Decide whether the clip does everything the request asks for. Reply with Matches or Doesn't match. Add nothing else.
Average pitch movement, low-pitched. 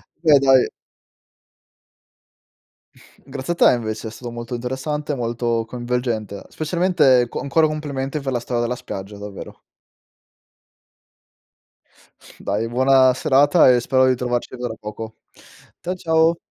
Matches